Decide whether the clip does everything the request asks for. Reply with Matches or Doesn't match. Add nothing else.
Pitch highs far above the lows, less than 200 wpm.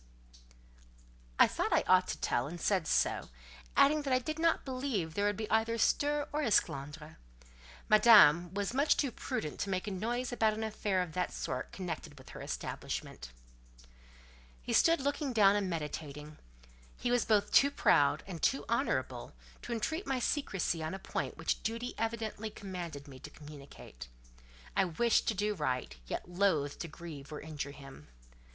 Matches